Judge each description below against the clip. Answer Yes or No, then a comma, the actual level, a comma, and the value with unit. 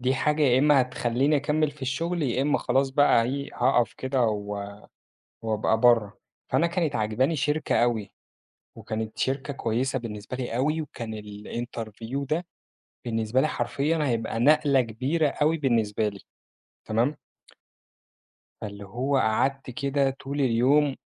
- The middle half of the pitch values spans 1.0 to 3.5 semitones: No, average, 4.1 semitones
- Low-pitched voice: Yes, low, 130 Hz